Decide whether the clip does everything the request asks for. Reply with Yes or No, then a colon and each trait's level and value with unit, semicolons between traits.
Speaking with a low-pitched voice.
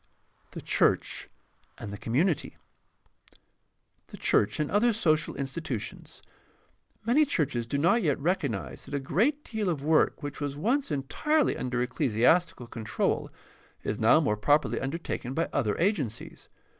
No: medium, 145 Hz